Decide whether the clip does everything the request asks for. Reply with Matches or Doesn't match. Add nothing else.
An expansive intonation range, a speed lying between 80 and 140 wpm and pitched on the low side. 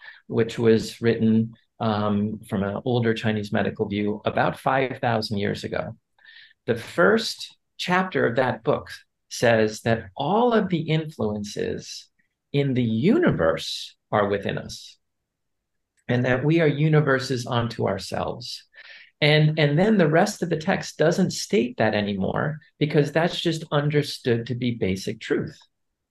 Matches